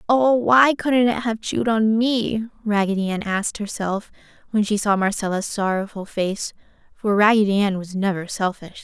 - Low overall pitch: No, high, 210 Hz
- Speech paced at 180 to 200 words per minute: No, average, 165 wpm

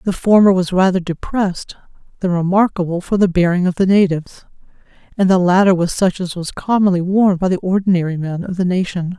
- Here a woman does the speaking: Yes, female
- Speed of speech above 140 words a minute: Yes, average, 190 wpm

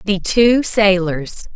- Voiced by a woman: Yes, female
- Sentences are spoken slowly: Yes, slow, 115 wpm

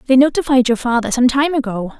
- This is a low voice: No, very high, 255 Hz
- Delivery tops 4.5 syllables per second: Yes, 6.2 syllables/s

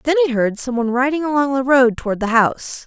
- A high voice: Yes, very high, 260 Hz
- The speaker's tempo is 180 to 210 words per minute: No, fast, 230 wpm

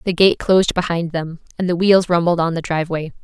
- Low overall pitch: No, medium, 170 Hz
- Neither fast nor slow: No, fast, 225 wpm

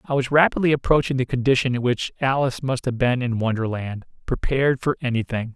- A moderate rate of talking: Yes, average, 175 wpm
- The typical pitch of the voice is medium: No, low, 130 Hz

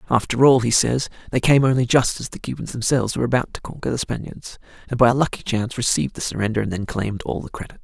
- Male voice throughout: Yes, male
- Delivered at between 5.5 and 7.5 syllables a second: Yes, 6.9 syllables/s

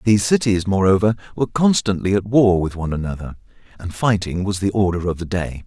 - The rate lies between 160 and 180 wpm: No, average, 190 wpm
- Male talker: Yes, male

